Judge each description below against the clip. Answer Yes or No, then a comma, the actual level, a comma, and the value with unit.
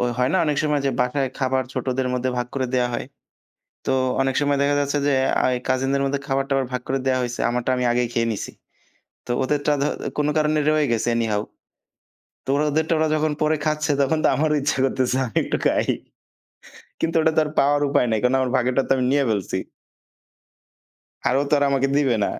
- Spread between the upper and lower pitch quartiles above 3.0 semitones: No, narrow, 2.6 semitones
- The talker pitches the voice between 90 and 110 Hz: No, low, 135 Hz